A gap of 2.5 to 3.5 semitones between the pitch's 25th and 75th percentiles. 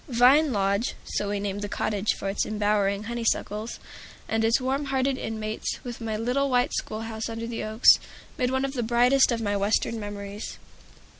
Yes: average, 3.2 semitones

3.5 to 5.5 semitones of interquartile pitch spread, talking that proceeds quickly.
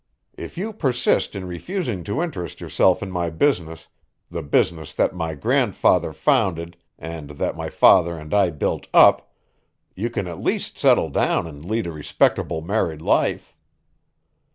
No: average, 4.2 semitones; average, 155 wpm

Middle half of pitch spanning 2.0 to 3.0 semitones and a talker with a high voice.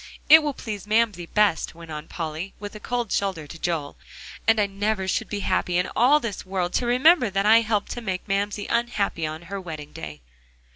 No: average, 4.4 semitones; high, 200 Hz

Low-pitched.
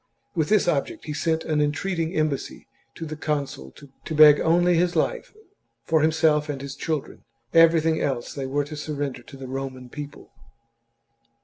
No: medium, 150 Hz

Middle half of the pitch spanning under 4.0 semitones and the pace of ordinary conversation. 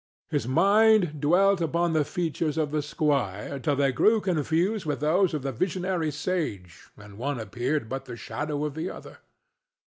No: average, 4.4 semitones; average, 170 wpm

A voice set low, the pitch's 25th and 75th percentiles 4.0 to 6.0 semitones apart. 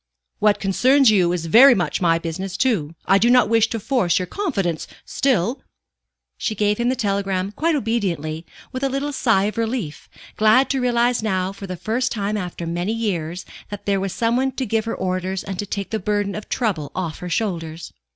No: high, 205 Hz; average, 4.5 semitones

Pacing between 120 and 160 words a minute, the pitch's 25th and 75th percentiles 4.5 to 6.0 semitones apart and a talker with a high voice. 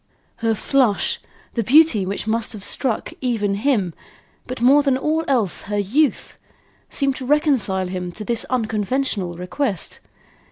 Yes: average, 145 wpm; average, 5.2 semitones; high, 230 Hz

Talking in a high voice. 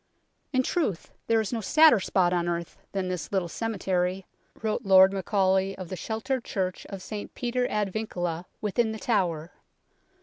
Yes: high, 195 Hz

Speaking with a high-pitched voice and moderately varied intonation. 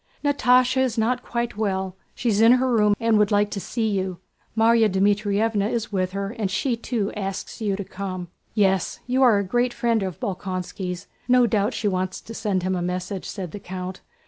Yes: high, 205 Hz; average, 3.4 semitones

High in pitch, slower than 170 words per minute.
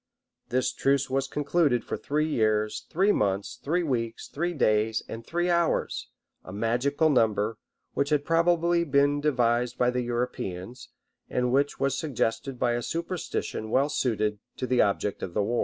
No: low, 130 Hz; average, 160 wpm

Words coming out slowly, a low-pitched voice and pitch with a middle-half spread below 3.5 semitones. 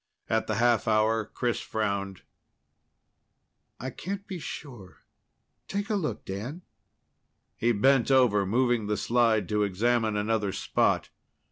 No: slow, 125 wpm; low, 115 Hz; average, 3.8 semitones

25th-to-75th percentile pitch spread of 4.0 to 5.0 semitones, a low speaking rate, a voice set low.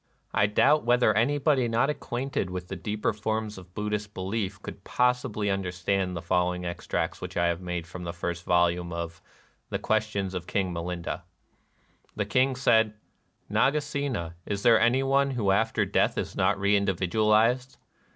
No: average, 4.7 semitones; average, 165 wpm; low, 100 Hz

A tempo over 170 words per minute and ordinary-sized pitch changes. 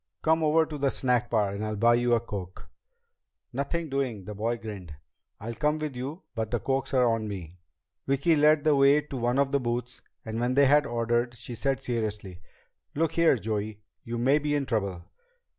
Yes: average, 200 wpm; average, 4.3 semitones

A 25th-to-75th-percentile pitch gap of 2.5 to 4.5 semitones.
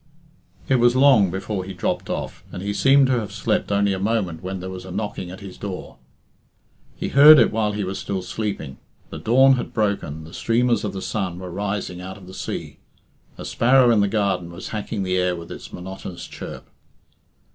Yes: average, 3.5 semitones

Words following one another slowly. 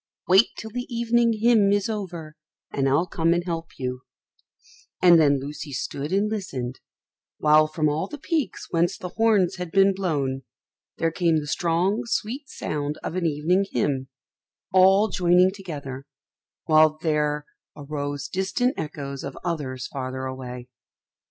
No: average, 145 wpm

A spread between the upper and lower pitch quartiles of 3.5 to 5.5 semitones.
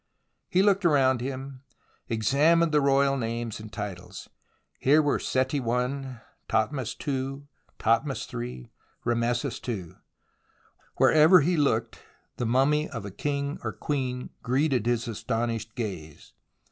Yes: average, 3.8 semitones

